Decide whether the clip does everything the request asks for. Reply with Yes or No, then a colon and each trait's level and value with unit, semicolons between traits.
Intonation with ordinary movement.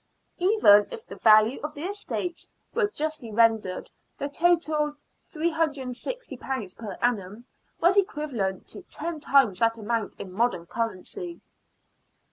No: wide, 7.2 semitones